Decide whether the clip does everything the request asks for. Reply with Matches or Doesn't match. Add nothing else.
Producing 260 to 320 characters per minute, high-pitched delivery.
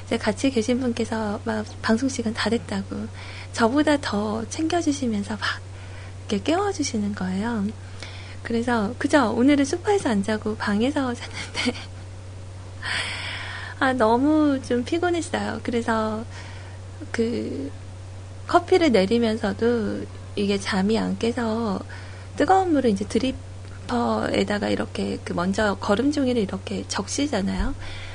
Doesn't match